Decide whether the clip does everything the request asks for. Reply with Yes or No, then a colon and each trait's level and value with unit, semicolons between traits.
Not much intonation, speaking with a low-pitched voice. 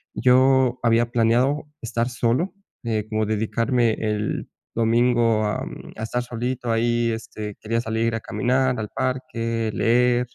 Yes: narrow, 1.6 semitones; low, 115 Hz